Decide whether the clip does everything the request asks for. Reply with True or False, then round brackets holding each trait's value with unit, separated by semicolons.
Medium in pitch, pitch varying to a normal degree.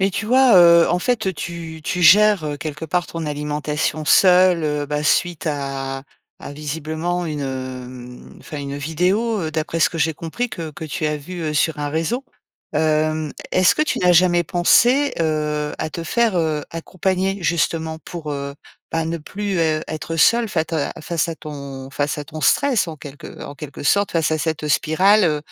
True (160 Hz; 3.1 semitones)